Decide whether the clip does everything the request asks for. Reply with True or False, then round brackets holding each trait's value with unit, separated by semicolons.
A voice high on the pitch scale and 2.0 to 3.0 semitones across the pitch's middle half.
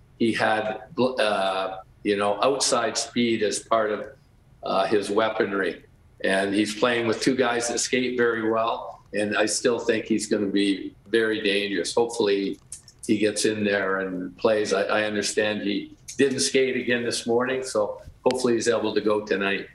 False (110 Hz; 2.7 semitones)